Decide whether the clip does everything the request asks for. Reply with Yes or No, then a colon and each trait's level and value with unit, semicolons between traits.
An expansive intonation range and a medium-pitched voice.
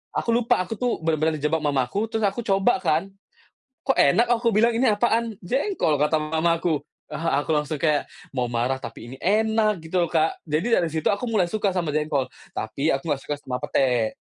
Yes: wide, 6.6 semitones; medium, 165 Hz